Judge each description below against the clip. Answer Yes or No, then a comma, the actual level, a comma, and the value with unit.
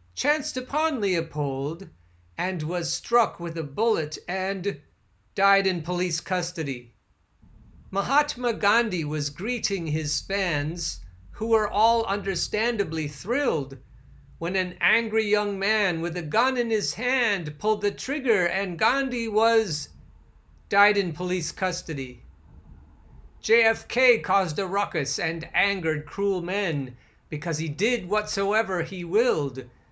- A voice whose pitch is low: No, medium, 185 Hz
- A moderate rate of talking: No, slow, 120 wpm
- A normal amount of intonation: No, wide, 6.3 semitones